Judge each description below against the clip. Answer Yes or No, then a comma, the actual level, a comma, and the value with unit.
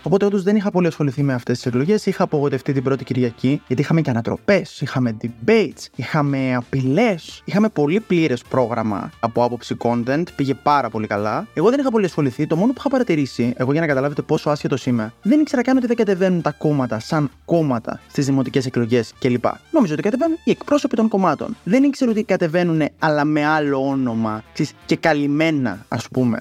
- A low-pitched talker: No, medium, 145 Hz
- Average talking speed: No, fast, 190 wpm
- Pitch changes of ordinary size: No, wide, 6.6 semitones